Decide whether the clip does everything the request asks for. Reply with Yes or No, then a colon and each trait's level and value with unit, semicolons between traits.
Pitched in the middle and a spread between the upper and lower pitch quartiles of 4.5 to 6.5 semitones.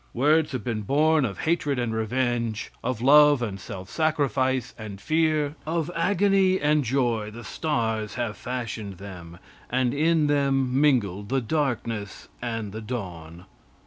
No: low, 125 Hz; wide, 5.5 semitones